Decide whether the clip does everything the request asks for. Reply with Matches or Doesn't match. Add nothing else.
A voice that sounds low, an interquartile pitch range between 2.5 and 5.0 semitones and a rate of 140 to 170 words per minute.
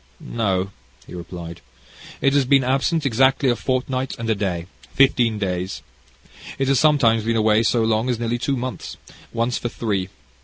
Matches